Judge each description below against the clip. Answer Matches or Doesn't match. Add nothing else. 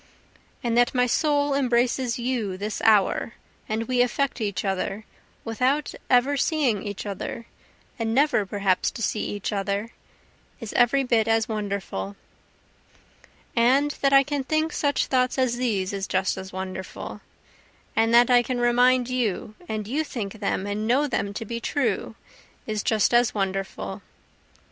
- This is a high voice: Matches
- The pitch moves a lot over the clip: Doesn't match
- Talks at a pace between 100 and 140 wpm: Doesn't match